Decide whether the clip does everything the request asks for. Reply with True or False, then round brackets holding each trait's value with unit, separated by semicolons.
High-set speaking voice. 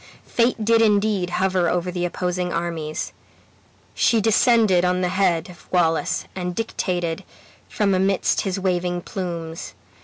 False (180 Hz)